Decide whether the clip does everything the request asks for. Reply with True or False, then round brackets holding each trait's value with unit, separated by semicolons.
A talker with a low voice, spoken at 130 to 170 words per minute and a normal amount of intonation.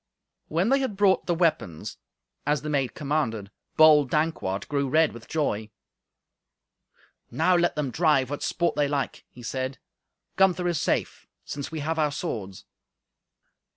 False (150 Hz; 150 wpm; 4.0 semitones)